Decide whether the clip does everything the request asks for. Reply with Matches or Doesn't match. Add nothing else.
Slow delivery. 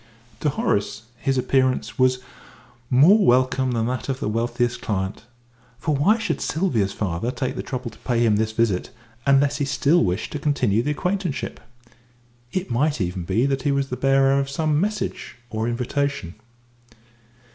Doesn't match